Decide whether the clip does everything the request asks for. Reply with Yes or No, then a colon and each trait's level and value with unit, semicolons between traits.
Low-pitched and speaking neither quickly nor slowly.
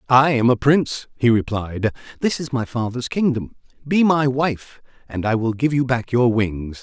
Yes: low, 125 Hz; average, 195 wpm